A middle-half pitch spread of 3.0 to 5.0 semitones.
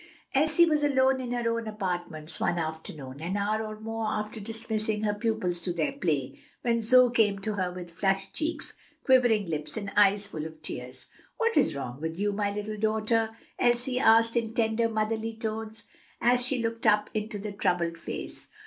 Yes: average, 3.8 semitones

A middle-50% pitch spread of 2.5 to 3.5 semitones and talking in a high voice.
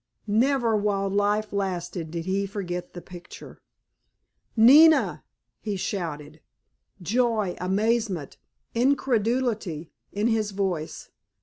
No: average, 4.1 semitones; high, 200 Hz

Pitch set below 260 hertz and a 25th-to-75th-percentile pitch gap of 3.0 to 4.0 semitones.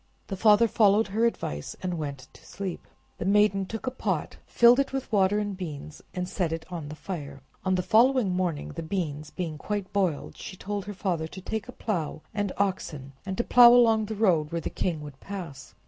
No: high, 190 Hz; average, 4.6 semitones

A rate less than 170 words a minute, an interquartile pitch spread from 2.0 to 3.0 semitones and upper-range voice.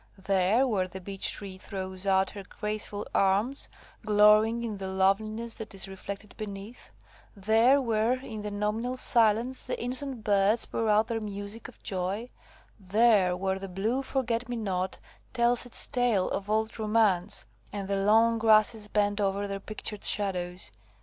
Yes: average, 155 wpm; average, 2.7 semitones; high, 210 Hz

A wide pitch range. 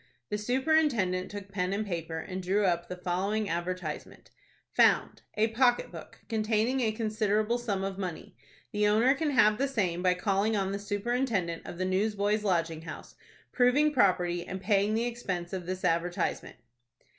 No: average, 3.5 semitones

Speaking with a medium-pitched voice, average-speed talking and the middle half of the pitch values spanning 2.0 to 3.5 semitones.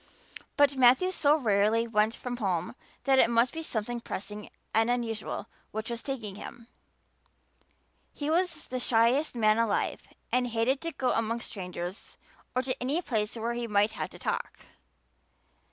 No: high, 235 Hz; average, 165 wpm; average, 3.0 semitones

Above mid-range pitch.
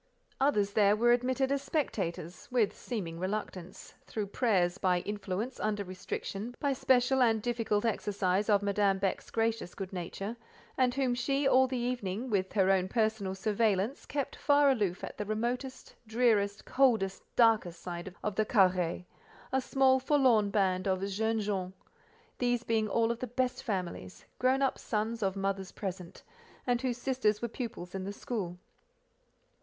Yes: high, 215 Hz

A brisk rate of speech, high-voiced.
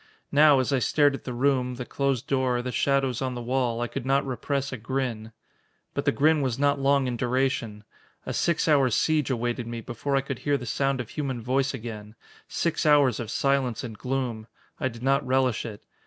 No: fast, 210 wpm; low, 130 Hz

